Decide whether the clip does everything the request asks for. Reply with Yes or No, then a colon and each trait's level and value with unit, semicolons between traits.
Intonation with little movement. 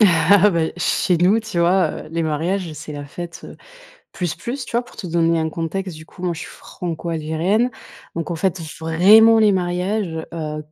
No: average, 3.1 semitones